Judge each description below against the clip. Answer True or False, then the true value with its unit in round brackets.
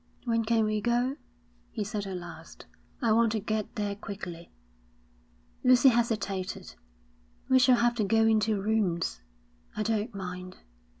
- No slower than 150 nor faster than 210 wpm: False (140 wpm)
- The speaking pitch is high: True (215 Hz)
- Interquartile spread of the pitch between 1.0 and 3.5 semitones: True (2.8 semitones)